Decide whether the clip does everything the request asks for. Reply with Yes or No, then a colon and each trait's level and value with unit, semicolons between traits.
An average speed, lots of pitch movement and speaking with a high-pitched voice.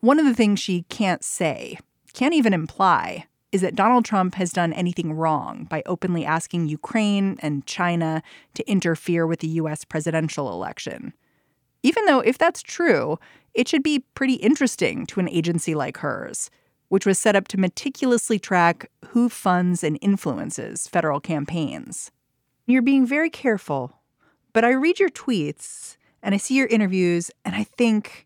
Yes: average, 160 wpm; wide, 6.5 semitones; high, 195 Hz